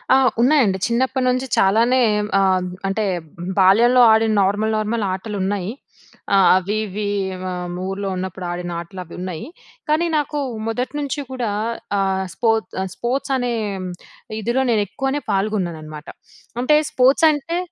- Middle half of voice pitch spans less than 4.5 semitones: No, average, 5.1 semitones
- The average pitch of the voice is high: Yes, high, 215 Hz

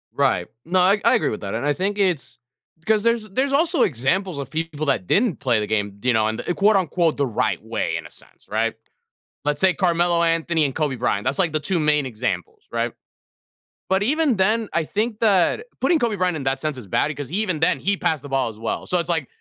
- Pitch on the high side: No, medium, 165 Hz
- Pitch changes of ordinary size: No, wide, 6.8 semitones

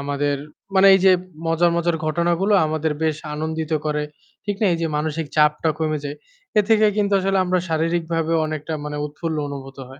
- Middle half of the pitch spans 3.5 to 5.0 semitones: No, narrow, 2.5 semitones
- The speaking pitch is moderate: Yes, medium, 160 Hz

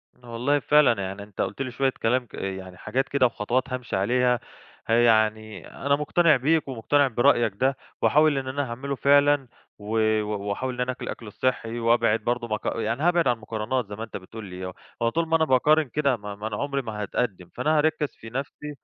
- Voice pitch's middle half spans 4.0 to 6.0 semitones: Yes, average, 4.4 semitones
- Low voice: Yes, low, 125 Hz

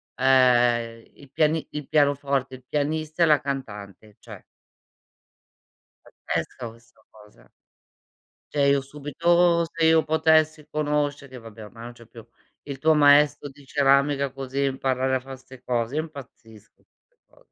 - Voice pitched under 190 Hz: Yes, medium, 140 Hz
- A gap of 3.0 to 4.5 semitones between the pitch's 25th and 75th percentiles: Yes, average, 3.3 semitones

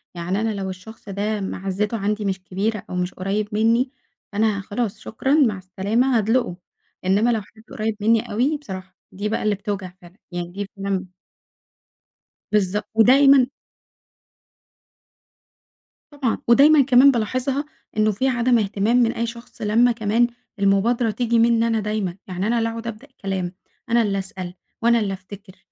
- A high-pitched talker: Yes, high, 215 Hz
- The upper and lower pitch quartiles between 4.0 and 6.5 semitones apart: No, average, 3.2 semitones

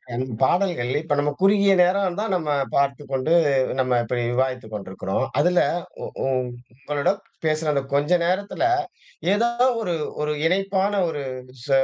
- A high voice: No, medium, 150 Hz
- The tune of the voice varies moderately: No, wide, 6.1 semitones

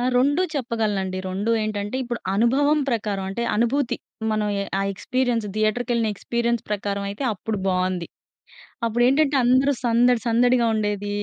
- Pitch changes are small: No, average, 3.3 semitones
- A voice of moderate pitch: No, high, 230 Hz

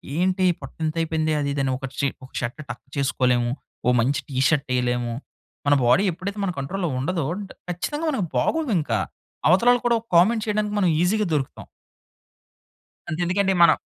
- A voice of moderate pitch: Yes, medium, 165 Hz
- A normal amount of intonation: No, wide, 6.3 semitones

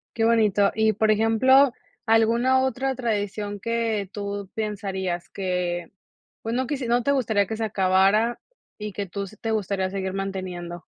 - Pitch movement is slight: No, average, 3.1 semitones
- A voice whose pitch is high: Yes, high, 210 Hz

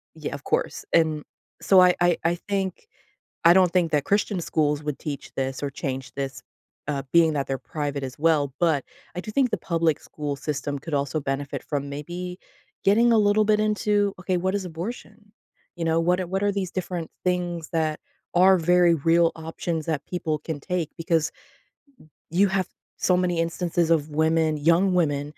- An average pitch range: Yes, average, 3.5 semitones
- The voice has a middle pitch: Yes, medium, 165 Hz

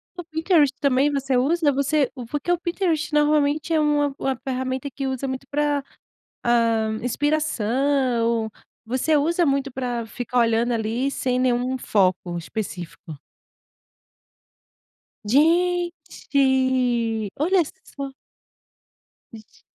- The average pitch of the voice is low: No, very high, 265 Hz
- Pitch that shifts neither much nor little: Yes, average, 3.8 semitones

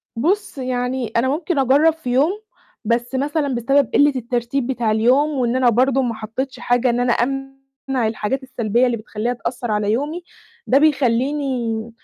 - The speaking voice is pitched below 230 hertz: No, very high, 255 Hz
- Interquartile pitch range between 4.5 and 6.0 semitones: No, narrow, 2.6 semitones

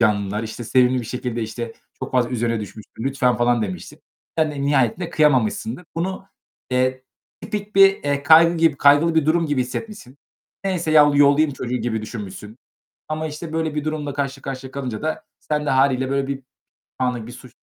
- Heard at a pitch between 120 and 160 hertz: Yes, low, 135 Hz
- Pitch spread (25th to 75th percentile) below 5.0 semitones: Yes, average, 4.2 semitones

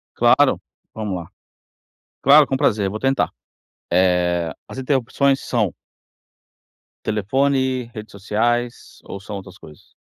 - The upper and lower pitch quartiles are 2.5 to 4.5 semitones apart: No, wide, 5.5 semitones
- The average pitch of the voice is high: No, low, 110 Hz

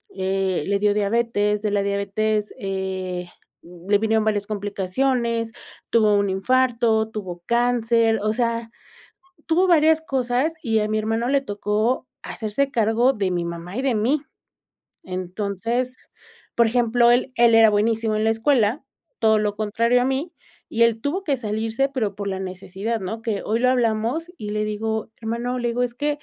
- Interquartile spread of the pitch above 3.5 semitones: No, average, 2.9 semitones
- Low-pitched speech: No, high, 220 Hz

